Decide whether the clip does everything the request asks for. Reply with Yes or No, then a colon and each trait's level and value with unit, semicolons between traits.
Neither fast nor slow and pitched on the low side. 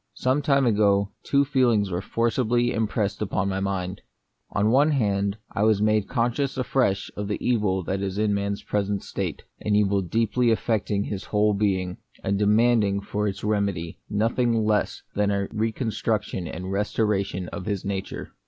Yes: average, 170 wpm; low, 105 Hz